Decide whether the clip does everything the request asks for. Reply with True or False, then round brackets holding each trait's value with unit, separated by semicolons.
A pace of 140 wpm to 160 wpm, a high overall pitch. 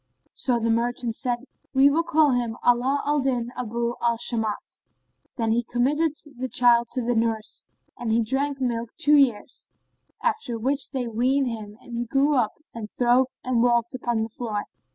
False (175 wpm; 240 Hz)